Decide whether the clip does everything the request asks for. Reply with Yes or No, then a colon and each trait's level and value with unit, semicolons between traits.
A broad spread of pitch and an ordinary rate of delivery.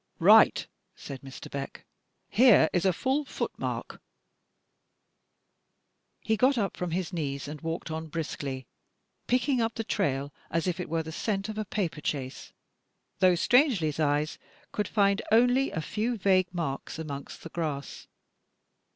Yes: wide, 6.0 semitones; average, 150 wpm